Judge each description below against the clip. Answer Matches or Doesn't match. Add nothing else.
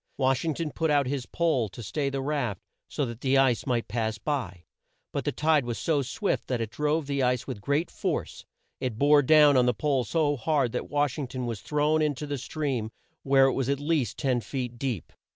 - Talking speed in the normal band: Doesn't match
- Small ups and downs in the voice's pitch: Doesn't match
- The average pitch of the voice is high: Doesn't match